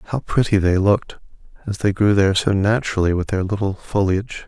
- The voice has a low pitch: Yes, low, 100 Hz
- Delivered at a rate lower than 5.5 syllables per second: No, 5.9 syllables/s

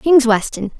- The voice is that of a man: No, female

